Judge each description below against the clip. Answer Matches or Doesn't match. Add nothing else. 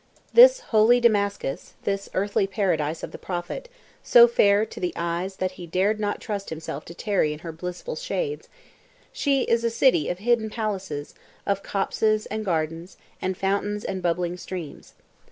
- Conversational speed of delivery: Matches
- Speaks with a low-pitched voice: Doesn't match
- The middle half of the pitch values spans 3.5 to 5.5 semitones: Matches